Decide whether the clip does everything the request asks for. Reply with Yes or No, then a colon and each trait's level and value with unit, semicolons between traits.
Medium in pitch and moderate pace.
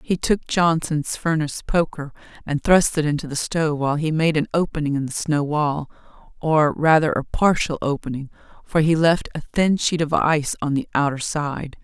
Yes: medium, 155 Hz; average, 190 wpm